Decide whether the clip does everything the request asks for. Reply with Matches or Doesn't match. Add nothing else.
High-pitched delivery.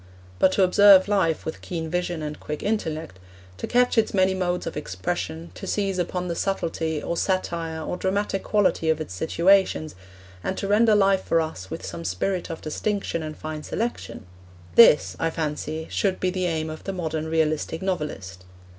Doesn't match